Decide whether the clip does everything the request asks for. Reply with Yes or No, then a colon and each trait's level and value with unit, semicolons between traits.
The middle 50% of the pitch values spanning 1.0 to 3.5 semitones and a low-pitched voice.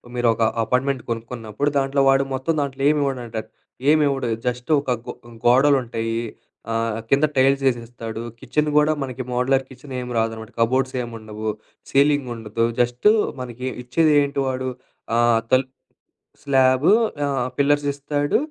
Yes: average, 2.9 semitones; low, 130 Hz